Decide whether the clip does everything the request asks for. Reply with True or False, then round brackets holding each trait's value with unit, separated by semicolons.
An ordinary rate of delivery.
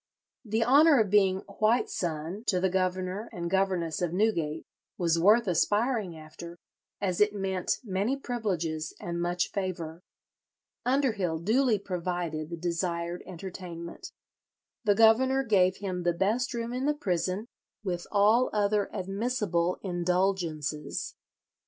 False (125 wpm)